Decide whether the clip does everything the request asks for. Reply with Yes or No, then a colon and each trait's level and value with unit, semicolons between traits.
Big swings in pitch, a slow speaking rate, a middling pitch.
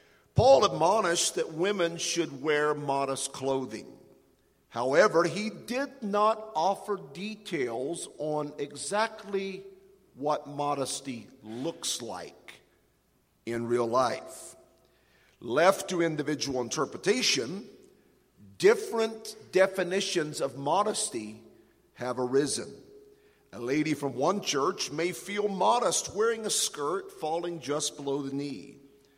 Yes: wide, 6.6 semitones; slow, 100 wpm; medium, 160 Hz